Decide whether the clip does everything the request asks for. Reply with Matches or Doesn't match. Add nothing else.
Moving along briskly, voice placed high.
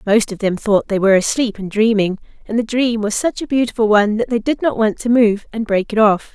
Matches